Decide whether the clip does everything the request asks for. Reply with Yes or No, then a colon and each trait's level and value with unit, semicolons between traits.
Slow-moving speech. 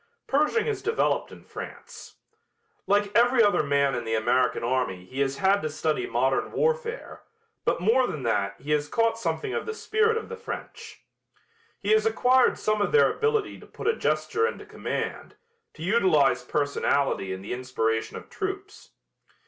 No: average, 170 wpm